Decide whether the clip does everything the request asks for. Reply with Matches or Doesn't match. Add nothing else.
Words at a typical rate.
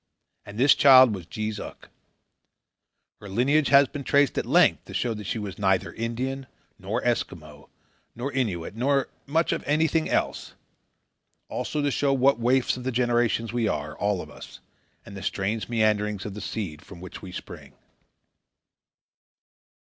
Matches